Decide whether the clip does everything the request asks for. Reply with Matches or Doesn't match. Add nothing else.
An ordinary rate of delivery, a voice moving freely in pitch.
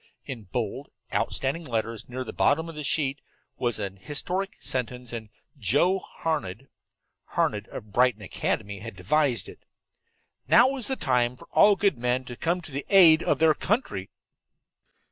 Matches